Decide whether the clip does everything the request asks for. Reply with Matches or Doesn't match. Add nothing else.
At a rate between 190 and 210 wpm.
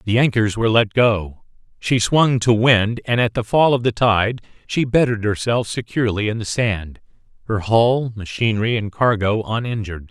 Doesn't match